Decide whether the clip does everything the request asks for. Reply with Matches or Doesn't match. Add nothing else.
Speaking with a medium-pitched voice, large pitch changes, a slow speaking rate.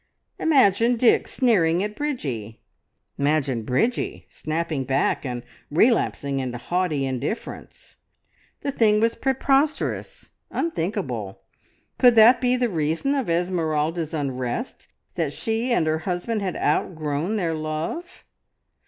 Matches